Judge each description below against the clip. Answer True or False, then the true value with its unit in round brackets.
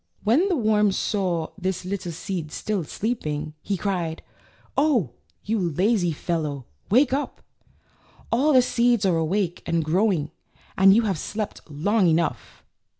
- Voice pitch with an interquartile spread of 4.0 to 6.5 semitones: True (4.9 semitones)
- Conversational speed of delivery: True (150 wpm)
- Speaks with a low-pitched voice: False (190 Hz)